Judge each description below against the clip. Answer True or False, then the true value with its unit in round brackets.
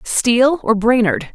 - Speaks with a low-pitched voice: False (225 Hz)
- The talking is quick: False (135 wpm)